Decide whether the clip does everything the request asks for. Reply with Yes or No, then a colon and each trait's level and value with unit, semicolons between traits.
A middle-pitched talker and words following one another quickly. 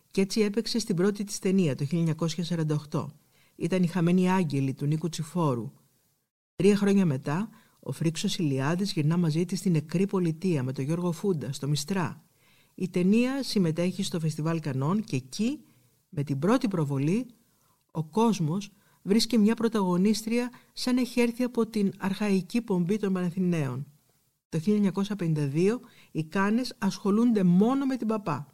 No: medium, 180 Hz; average, 145 wpm